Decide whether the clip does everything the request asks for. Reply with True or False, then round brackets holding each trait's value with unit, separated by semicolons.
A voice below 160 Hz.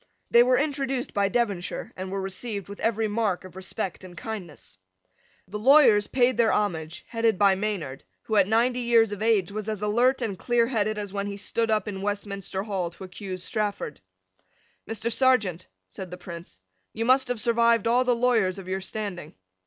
False (210 Hz)